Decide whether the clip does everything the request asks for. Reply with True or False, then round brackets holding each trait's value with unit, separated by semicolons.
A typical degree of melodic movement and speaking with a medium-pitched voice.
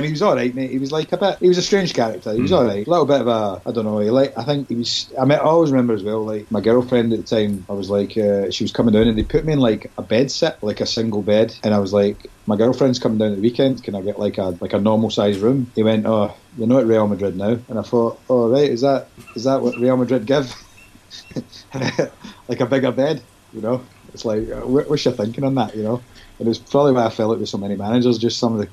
False (3.5 semitones; 115 Hz)